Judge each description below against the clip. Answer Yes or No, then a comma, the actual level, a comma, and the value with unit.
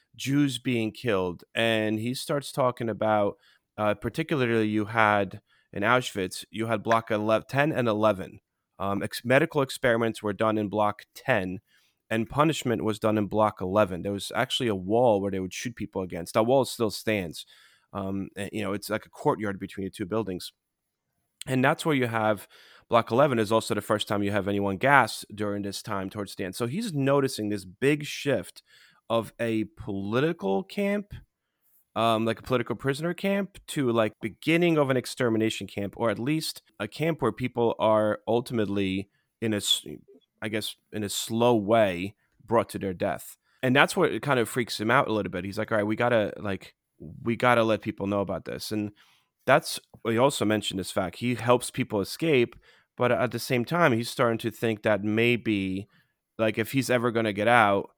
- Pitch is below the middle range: Yes, low, 110 Hz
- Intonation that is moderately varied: Yes, average, 3.3 semitones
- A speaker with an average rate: Yes, average, 190 wpm